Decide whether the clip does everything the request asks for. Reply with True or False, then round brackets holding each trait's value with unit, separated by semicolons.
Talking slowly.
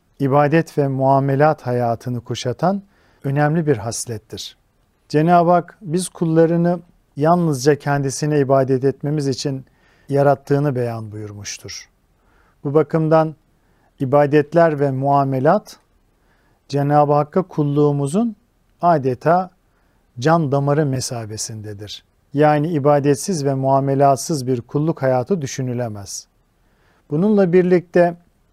True (90 wpm)